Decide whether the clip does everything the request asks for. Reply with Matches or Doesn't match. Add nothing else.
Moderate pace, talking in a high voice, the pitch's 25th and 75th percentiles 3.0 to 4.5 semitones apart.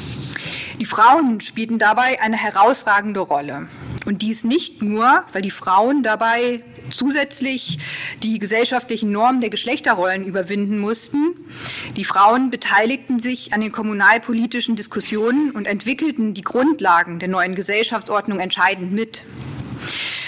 Doesn't match